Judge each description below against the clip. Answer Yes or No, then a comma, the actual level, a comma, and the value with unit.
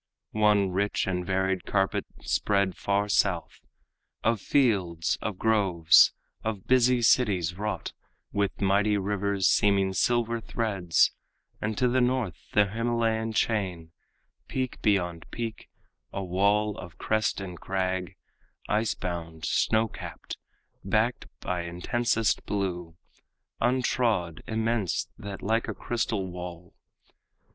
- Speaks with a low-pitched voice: Yes, low, 100 Hz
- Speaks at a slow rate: Yes, slow, 115 wpm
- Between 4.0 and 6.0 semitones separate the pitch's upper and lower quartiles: No, average, 3.5 semitones